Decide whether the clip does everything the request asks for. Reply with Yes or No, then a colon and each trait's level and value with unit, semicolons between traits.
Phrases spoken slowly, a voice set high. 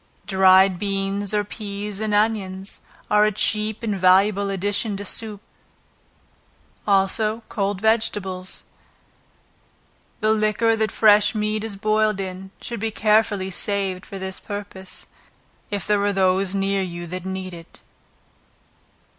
Yes: slow, 130 wpm; high, 200 Hz